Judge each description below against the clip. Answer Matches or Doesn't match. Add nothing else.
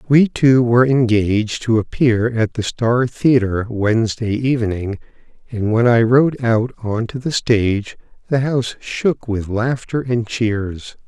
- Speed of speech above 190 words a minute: Doesn't match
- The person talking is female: Doesn't match